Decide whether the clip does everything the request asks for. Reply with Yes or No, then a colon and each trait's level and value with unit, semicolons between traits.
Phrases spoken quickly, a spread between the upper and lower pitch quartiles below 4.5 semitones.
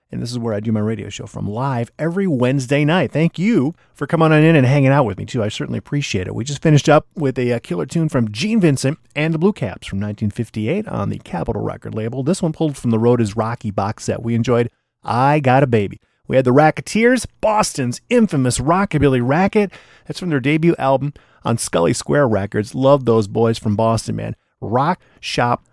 No: fast, 215 wpm; average, 5.2 semitones